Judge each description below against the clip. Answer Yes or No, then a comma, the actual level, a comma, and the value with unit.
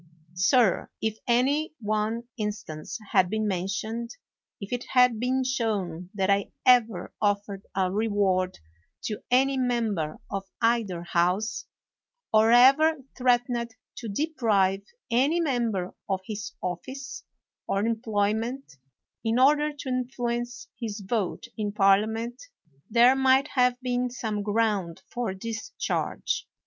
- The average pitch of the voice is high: Yes, high, 225 Hz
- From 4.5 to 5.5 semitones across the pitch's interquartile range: No, average, 3.8 semitones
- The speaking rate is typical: No, slow, 125 wpm